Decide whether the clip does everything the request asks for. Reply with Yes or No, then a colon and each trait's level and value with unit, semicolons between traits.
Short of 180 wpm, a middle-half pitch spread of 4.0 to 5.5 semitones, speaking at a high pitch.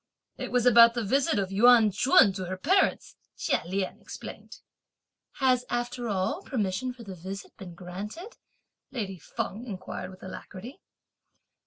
Yes: average, 145 wpm; average, 4.7 semitones; high, 210 Hz